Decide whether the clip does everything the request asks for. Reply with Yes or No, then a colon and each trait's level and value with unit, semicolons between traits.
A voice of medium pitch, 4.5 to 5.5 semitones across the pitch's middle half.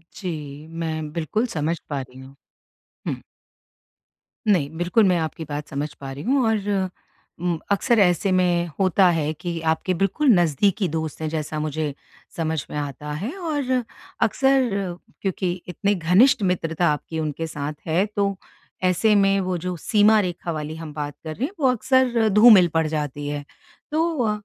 Yes: medium, 175 Hz; average, 5.0 semitones